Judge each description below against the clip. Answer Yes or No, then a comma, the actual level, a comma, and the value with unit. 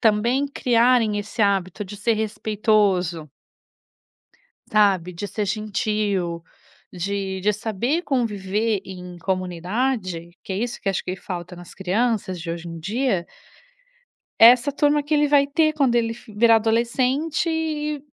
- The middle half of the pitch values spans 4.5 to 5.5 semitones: Yes, average, 4.8 semitones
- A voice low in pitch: No, high, 215 Hz